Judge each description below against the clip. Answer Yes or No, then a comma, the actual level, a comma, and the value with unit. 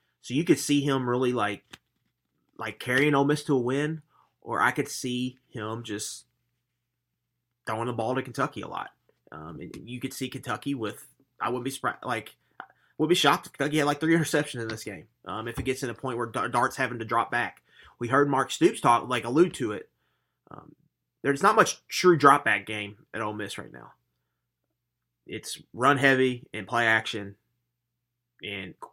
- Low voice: Yes, low, 125 Hz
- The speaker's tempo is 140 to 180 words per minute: No, average, 195 wpm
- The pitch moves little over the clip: No, average, 3.5 semitones